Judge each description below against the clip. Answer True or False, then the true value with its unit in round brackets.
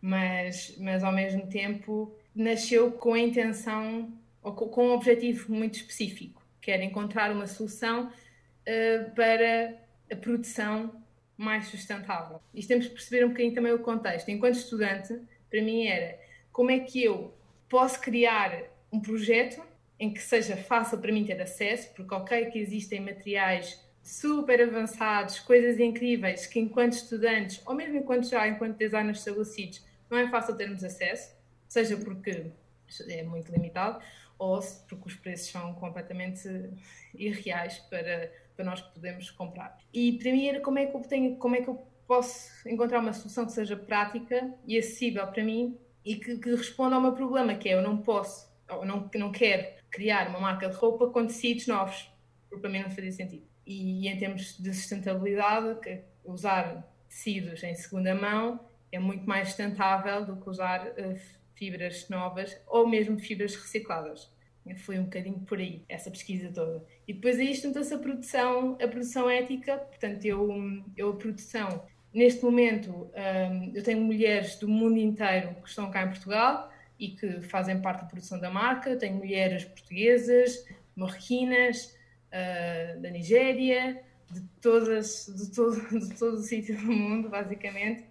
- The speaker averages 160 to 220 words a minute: True (165 wpm)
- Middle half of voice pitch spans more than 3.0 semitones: True (3.8 semitones)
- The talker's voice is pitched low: False (215 Hz)